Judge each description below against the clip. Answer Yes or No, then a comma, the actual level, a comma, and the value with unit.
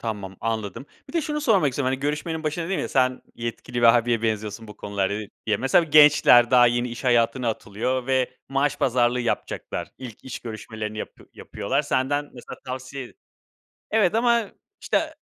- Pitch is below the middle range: Yes, low, 125 Hz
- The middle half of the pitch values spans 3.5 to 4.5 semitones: Yes, average, 4.1 semitones